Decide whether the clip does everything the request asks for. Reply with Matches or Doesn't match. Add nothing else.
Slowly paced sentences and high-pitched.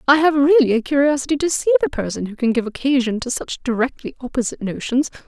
Doesn't match